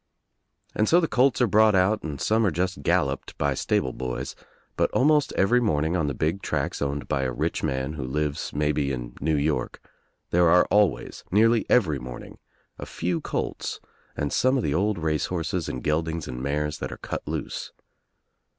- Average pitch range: No, wide, 6.4 semitones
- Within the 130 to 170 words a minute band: No, average, 185 wpm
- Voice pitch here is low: Yes, very low, 80 Hz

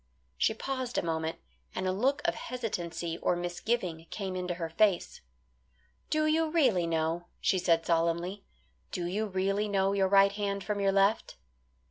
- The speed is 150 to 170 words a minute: Yes, average, 160 wpm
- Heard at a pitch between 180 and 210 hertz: Yes, high, 190 Hz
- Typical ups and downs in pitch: Yes, average, 3.5 semitones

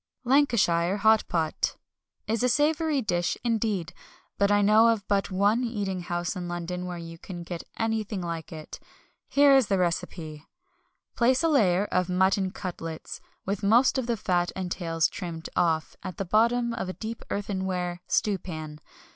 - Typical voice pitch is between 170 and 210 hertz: Yes, high, 190 Hz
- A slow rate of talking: No, average, 165 wpm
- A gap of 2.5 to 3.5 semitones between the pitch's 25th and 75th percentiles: No, average, 4.3 semitones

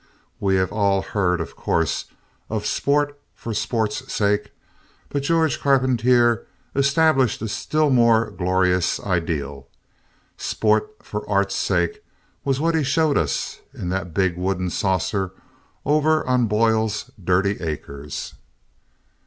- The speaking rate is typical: No, slow, 120 wpm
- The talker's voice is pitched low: Yes, low, 105 Hz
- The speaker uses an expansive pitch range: Yes, wide, 6.8 semitones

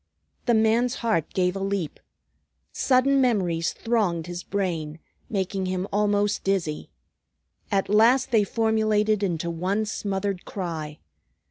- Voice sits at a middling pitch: No, high, 200 Hz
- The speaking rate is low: Yes, slow, 120 wpm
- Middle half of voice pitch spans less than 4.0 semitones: Yes, average, 3.4 semitones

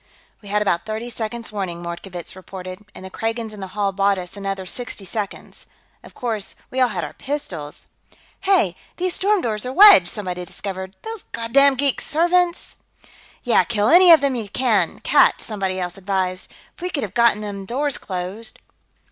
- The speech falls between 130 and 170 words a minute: No, average, 180 wpm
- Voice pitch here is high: Yes, high, 210 Hz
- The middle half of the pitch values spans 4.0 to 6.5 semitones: Yes, average, 5.2 semitones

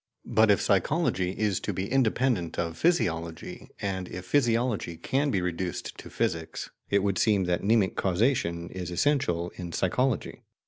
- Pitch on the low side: Yes, very low, 95 Hz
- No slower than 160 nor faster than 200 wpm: No, average, 150 wpm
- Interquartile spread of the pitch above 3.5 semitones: Yes, average, 4.9 semitones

